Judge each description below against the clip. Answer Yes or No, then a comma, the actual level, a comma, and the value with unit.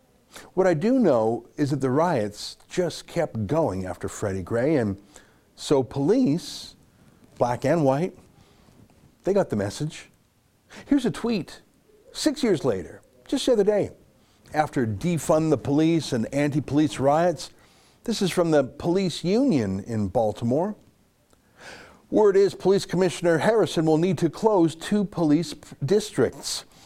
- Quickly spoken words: No, average, 140 wpm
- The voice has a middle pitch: Yes, medium, 155 Hz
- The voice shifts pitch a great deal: Yes, wide, 6.6 semitones